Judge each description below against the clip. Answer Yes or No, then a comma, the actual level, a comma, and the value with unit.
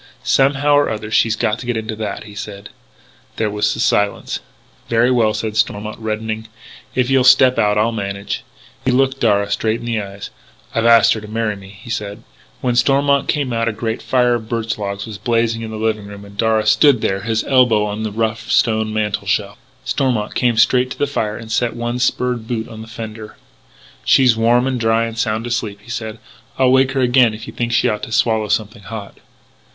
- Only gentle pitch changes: Yes, narrow, 2.2 semitones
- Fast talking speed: Yes, fast, 215 wpm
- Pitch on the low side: Yes, low, 110 Hz